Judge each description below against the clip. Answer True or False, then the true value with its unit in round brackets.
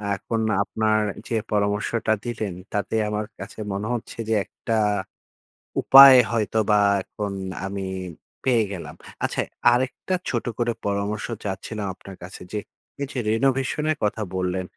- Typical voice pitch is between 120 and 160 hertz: False (110 Hz)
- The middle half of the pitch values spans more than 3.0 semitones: False (2.7 semitones)